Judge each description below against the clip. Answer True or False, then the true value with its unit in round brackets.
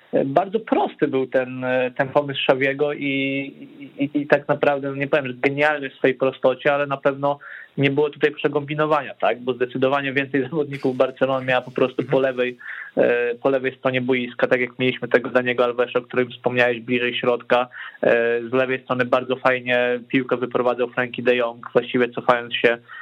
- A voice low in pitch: True (130 Hz)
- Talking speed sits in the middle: False (175 wpm)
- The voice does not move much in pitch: True (2.3 semitones)